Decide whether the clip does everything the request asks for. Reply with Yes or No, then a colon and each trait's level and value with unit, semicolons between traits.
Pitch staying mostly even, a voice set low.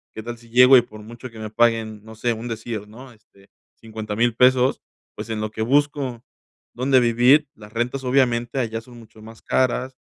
Yes: narrow, 2.3 semitones; low, 120 Hz